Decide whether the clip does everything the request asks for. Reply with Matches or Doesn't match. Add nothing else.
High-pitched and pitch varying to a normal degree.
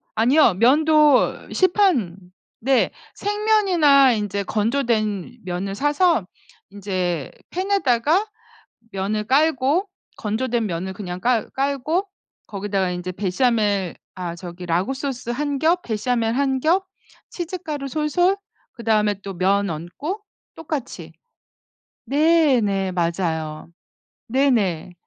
Doesn't match